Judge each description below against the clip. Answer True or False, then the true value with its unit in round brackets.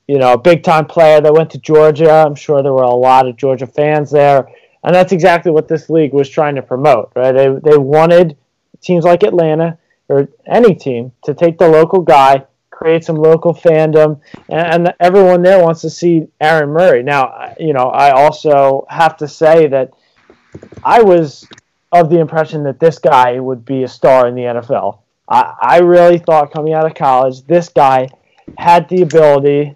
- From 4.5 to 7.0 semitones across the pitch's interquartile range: False (3.6 semitones)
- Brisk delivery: False (190 wpm)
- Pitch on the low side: False (155 Hz)